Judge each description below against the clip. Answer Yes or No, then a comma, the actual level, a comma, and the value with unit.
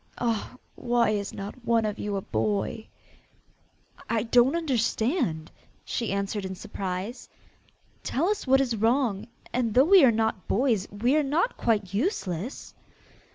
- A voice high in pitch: Yes, high, 230 Hz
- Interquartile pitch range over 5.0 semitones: No, average, 4.3 semitones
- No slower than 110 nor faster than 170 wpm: Yes, average, 145 wpm